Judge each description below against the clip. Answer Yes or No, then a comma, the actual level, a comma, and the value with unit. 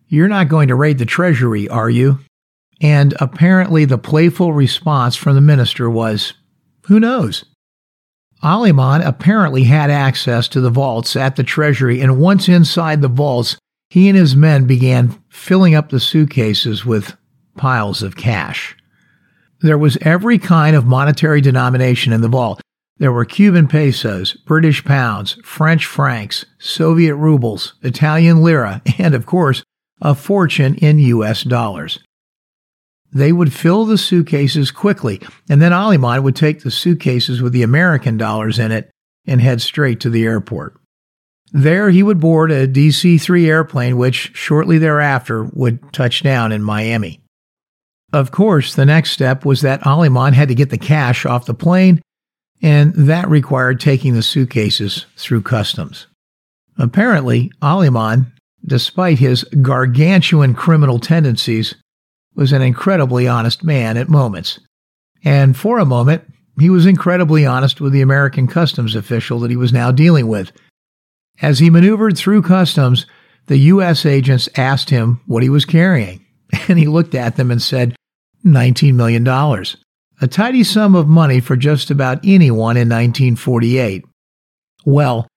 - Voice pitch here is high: No, medium, 140 Hz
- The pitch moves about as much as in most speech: Yes, average, 4.6 semitones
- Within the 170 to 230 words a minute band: No, average, 150 wpm